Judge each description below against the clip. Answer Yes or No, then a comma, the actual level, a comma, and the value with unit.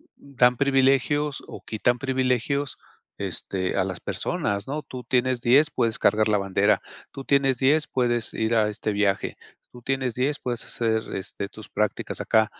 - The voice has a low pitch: Yes, low, 125 Hz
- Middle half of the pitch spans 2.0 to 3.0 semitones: No, average, 3.7 semitones